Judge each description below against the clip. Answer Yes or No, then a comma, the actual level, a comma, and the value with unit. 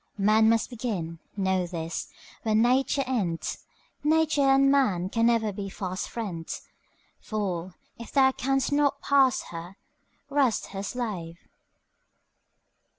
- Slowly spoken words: Yes, slow, 120 wpm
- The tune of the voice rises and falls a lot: Yes, wide, 6.2 semitones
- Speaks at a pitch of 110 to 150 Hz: No, high, 220 Hz